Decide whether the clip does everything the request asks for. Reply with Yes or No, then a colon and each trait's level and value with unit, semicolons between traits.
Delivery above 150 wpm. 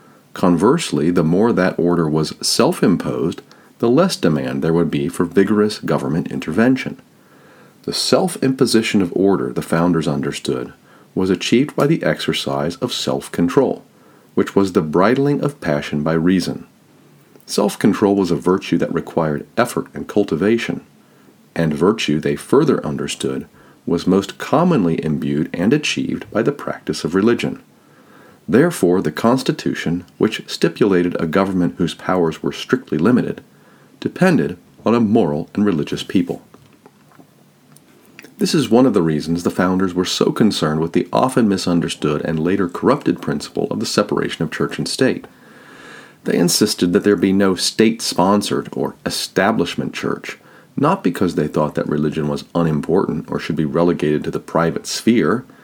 No: average, 145 wpm